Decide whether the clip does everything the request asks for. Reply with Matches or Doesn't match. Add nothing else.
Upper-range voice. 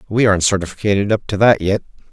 Doesn't match